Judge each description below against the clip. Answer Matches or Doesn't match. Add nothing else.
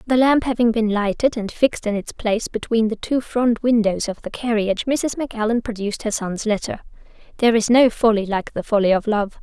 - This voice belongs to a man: Doesn't match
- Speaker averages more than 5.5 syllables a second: Matches